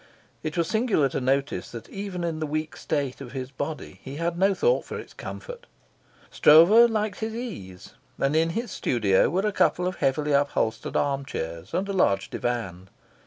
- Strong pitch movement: Yes, wide, 6.8 semitones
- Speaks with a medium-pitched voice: Yes, medium, 155 Hz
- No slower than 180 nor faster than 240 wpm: Yes, average, 185 wpm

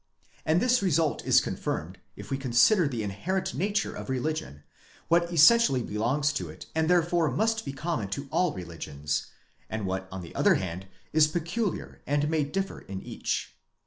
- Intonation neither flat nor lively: No, wide, 7.9 semitones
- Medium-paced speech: Yes, average, 170 wpm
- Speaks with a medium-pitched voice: Yes, medium, 150 Hz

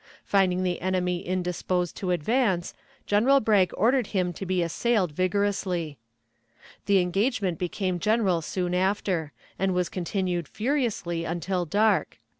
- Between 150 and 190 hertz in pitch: Yes, medium, 185 Hz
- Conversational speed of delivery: No, slow, 125 wpm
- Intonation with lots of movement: No, narrow, 2.5 semitones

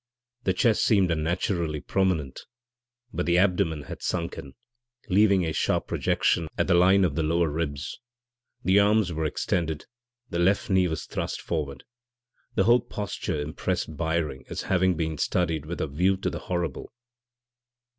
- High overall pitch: No, very low, 85 Hz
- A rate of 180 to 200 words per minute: No, average, 155 wpm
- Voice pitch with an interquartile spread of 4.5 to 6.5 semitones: No, average, 3.1 semitones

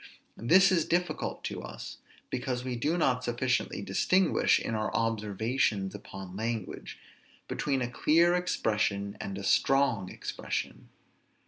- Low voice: Yes, low, 120 Hz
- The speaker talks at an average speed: No, slow, 125 wpm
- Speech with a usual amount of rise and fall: No, wide, 6.1 semitones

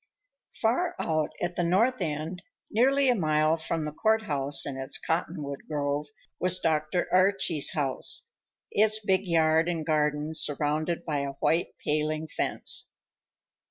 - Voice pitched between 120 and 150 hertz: No, medium, 160 Hz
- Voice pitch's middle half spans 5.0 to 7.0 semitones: No, average, 3.5 semitones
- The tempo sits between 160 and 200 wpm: No, average, 140 wpm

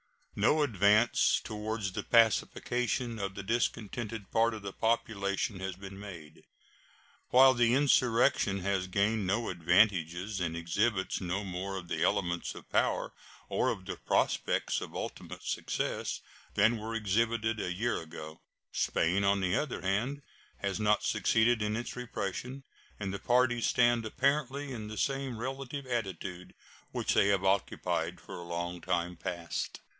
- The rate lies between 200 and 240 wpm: No, average, 150 wpm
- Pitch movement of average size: Yes, average, 3.9 semitones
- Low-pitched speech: Yes, low, 105 Hz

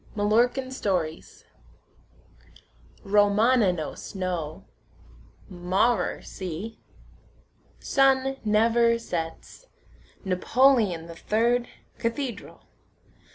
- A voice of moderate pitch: No, high, 215 Hz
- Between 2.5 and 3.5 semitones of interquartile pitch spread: No, average, 5.0 semitones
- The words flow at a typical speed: No, slow, 60 wpm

